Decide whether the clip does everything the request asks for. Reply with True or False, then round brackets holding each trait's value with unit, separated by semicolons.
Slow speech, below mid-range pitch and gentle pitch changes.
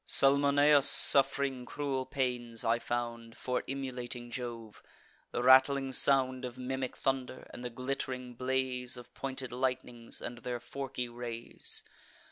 True (125 wpm; 125 Hz; 1.7 semitones)